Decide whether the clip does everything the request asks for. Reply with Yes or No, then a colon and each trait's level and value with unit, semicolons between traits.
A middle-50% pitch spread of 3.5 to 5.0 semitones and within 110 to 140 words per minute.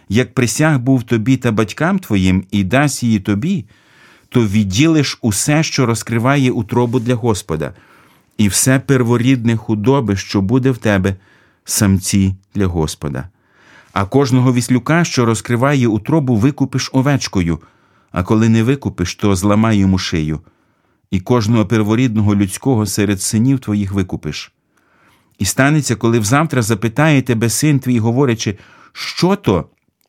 Yes: average, 4.5 semitones; average, 130 wpm